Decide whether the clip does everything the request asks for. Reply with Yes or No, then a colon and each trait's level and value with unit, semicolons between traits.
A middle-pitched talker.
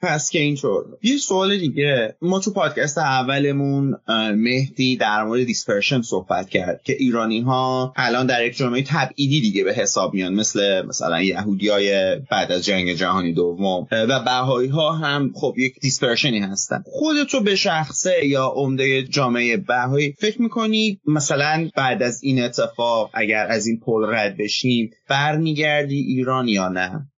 No: low, 130 Hz